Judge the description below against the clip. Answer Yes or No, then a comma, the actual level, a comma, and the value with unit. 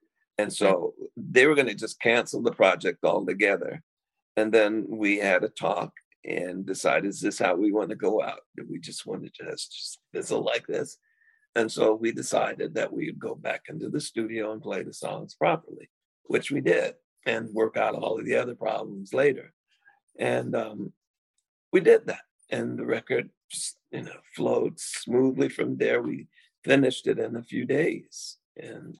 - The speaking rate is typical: Yes, average, 180 wpm